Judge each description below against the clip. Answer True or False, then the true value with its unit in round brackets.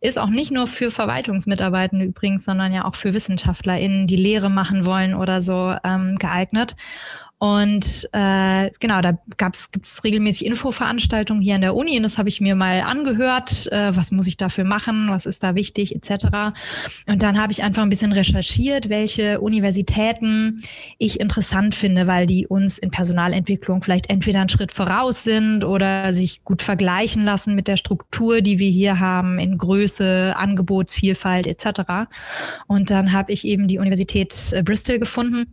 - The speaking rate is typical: True (170 wpm)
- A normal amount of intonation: False (2.0 semitones)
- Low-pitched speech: False (195 Hz)